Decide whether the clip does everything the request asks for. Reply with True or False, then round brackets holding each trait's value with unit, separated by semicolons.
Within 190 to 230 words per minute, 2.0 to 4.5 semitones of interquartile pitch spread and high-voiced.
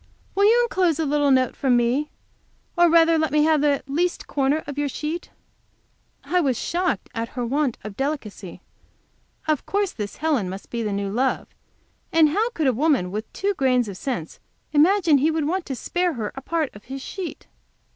False (195 wpm; 5.1 semitones; 290 Hz)